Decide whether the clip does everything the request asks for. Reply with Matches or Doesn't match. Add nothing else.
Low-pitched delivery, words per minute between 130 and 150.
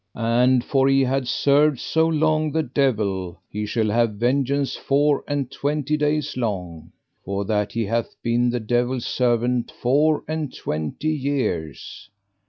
Matches